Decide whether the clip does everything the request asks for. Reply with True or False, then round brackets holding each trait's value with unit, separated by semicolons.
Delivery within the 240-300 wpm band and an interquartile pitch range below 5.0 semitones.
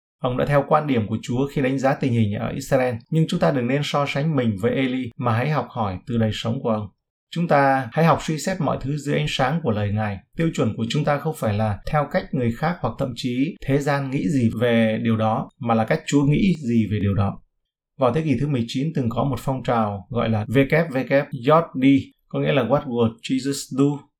True (245 wpm; 4.0 semitones)